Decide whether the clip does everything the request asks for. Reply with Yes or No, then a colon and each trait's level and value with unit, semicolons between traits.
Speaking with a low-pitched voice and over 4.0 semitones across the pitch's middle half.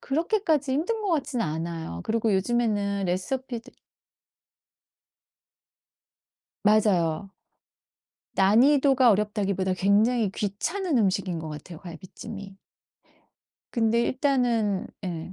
No: high, 210 Hz; wide, 5.4 semitones